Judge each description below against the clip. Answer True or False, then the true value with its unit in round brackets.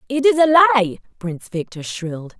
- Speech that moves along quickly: False (175 wpm)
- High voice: True (225 Hz)